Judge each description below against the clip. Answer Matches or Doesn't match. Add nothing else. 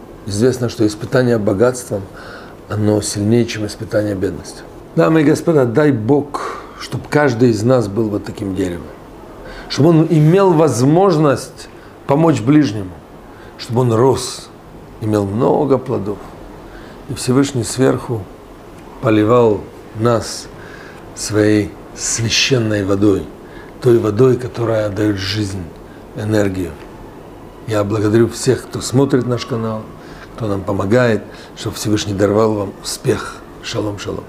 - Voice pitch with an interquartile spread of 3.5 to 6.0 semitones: Matches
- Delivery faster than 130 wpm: Doesn't match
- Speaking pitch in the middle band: Doesn't match